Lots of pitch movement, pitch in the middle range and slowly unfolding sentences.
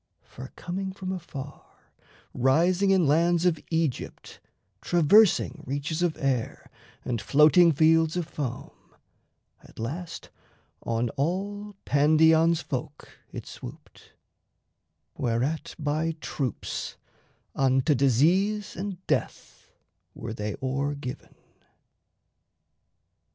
No: average, 4.5 semitones; medium, 155 Hz; slow, 95 wpm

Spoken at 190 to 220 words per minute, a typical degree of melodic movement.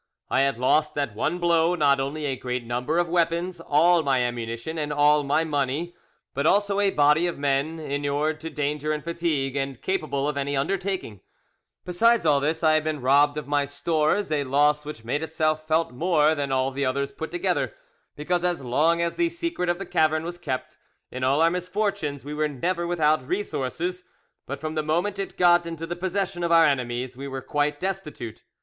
Yes: average, 195 wpm; average, 3.6 semitones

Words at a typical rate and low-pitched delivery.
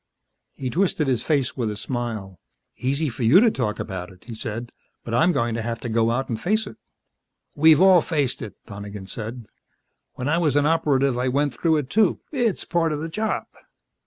No: fast, 210 wpm; low, 130 Hz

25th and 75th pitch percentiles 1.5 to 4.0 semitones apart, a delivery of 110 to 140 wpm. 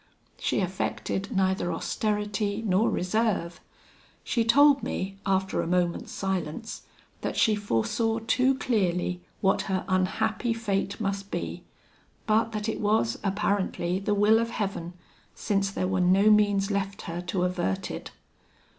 Yes: average, 2.7 semitones; slow, 135 wpm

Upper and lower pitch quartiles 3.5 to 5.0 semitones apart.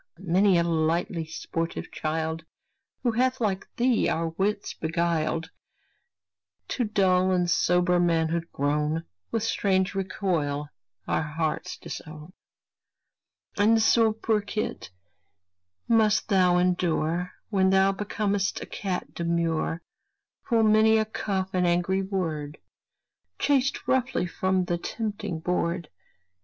Yes: average, 3.9 semitones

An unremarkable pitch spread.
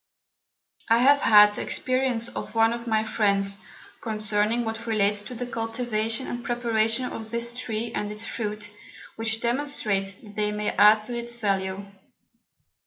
No: narrow, 2.2 semitones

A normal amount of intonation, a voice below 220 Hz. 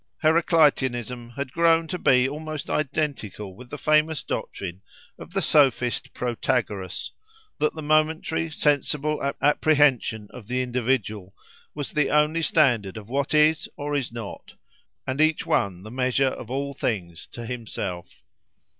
Yes: average, 4.5 semitones; low, 135 Hz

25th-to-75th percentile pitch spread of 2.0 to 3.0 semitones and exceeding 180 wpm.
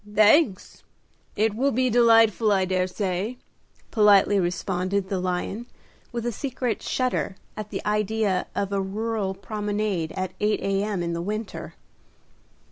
No: average, 2.7 semitones; slow, 135 wpm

